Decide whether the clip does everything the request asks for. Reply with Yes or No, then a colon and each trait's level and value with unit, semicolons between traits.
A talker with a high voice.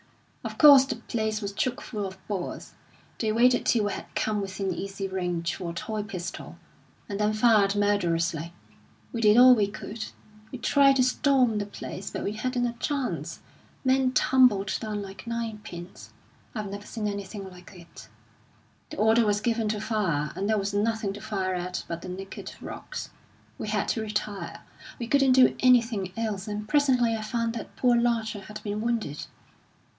Yes: high, 215 Hz